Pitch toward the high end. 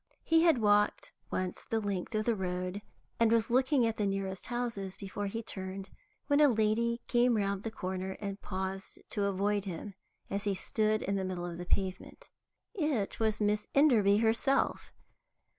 Yes: high, 205 Hz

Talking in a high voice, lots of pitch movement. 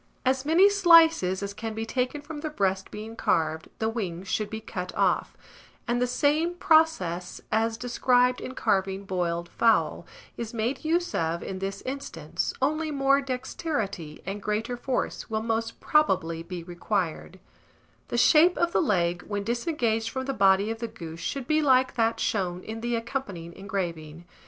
Yes: high, 225 Hz; wide, 5.9 semitones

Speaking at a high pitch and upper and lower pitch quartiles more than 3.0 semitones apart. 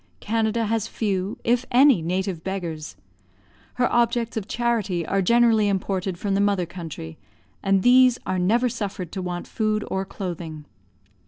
Yes: high, 200 Hz; average, 4.1 semitones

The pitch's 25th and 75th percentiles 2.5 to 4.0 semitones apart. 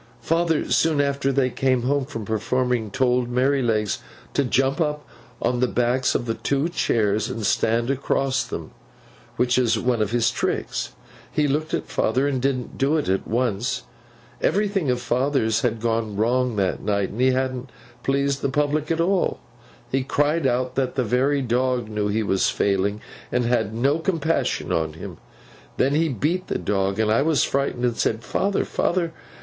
Yes: average, 3.7 semitones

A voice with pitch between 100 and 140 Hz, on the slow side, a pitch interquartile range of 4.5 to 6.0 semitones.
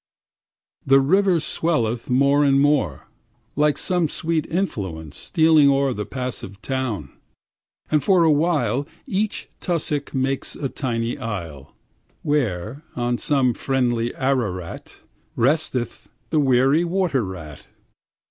Yes: low, 135 Hz; slow, 115 wpm; average, 4.8 semitones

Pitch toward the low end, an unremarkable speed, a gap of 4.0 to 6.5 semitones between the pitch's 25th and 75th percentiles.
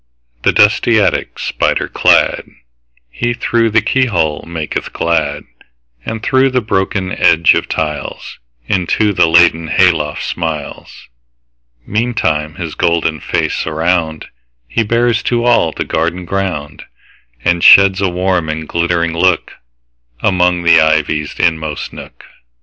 No: very low, 80 Hz; slow, 110 wpm; average, 4.6 semitones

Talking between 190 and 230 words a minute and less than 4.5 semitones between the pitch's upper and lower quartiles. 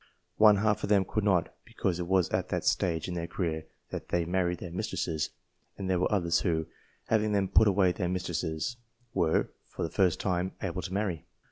Yes: fast, 205 wpm; narrow, 2.4 semitones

